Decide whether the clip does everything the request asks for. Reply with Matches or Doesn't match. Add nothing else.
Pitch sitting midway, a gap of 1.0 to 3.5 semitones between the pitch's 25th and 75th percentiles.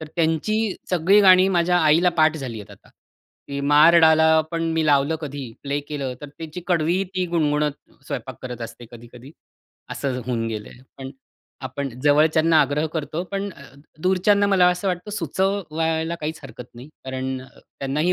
Doesn't match